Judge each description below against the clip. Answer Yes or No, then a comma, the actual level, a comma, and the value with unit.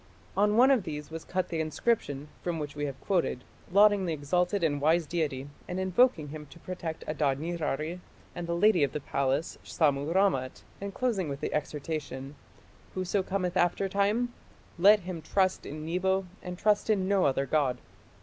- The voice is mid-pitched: Yes, medium, 170 Hz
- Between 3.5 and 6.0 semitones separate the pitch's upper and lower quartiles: Yes, average, 4.5 semitones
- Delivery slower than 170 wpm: No, average, 180 wpm